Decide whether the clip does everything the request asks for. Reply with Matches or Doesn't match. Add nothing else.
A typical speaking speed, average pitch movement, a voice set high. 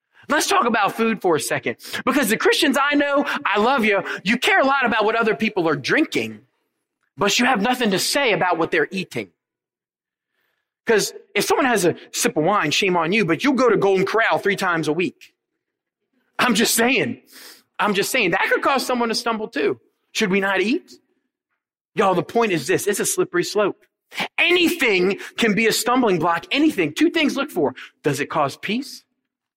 Doesn't match